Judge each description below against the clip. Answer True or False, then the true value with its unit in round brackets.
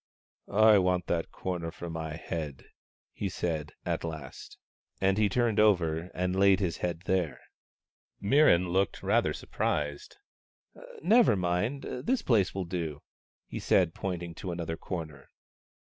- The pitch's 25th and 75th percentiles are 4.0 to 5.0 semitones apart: False (3.2 semitones)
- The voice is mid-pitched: False (90 Hz)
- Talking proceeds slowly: False (150 wpm)